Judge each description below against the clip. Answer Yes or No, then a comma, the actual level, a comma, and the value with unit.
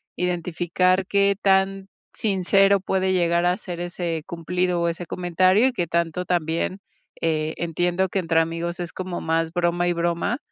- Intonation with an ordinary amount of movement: No, narrow, 1.7 semitones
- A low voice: No, medium, 175 Hz